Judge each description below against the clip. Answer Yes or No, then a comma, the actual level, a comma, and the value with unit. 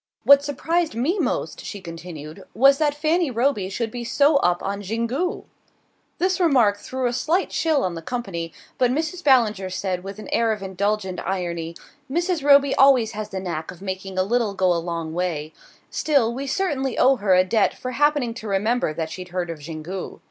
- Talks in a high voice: Yes, high, 220 Hz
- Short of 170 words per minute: No, average, 190 wpm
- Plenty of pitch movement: Yes, wide, 7.0 semitones